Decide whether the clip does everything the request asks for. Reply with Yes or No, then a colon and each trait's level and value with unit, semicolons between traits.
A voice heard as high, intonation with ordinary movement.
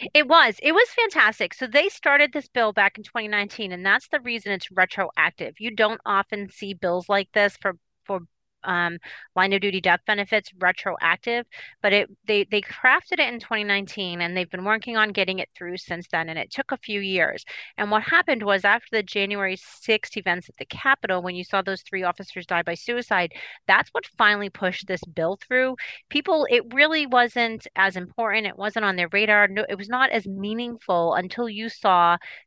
Yes: high, 205 Hz; average, 4.0 semitones